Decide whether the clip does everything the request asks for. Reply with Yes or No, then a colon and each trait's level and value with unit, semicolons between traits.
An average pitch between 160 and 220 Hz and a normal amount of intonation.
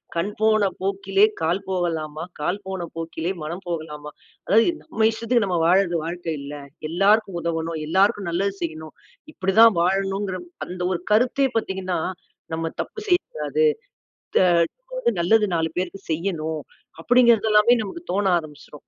Yes: medium, 185 Hz; average, 4.1 semitones